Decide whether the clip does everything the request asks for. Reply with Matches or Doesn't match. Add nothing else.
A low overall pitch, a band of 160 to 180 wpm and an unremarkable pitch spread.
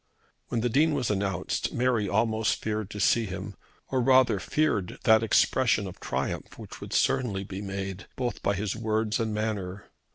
Matches